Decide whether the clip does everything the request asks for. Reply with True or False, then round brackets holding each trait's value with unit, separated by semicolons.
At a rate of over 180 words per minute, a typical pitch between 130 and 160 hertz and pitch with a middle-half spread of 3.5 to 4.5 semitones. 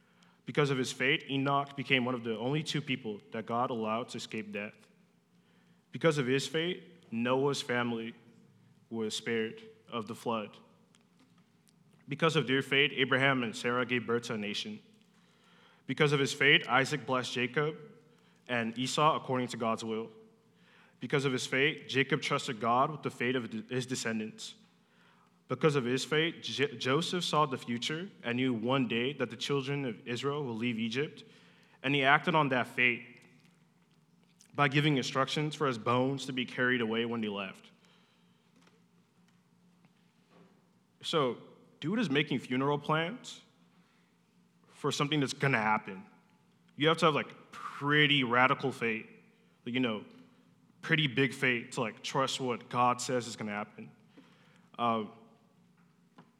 False (155 wpm; 135 Hz; 4.1 semitones)